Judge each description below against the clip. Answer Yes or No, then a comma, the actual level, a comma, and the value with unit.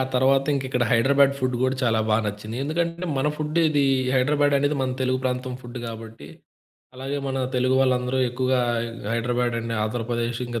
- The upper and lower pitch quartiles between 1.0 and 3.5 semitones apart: Yes, narrow, 2.5 semitones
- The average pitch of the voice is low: Yes, low, 130 Hz